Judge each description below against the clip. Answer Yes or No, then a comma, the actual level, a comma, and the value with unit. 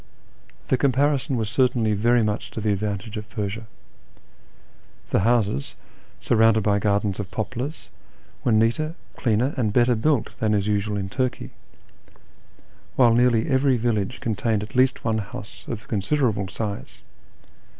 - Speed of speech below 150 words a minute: Yes, average, 140 wpm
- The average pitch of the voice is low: Yes, low, 110 Hz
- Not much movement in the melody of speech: No, average, 3.0 semitones